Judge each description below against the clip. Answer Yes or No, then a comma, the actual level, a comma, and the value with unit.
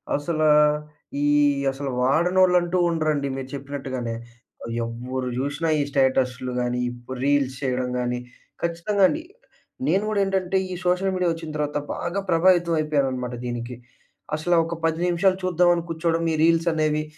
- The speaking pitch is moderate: Yes, medium, 155 Hz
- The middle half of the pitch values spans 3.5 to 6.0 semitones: Yes, average, 4.7 semitones